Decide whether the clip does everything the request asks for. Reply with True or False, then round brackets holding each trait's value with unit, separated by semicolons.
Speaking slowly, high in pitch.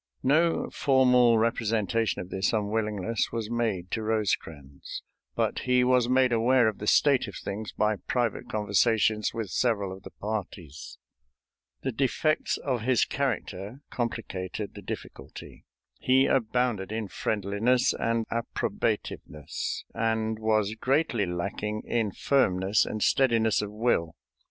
False (125 wpm; 110 Hz)